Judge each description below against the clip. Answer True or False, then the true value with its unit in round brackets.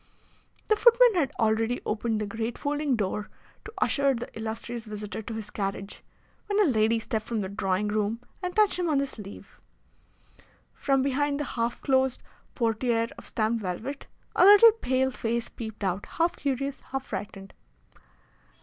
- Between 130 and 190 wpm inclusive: True (160 wpm)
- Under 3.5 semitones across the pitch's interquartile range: False (4.6 semitones)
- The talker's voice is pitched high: True (235 Hz)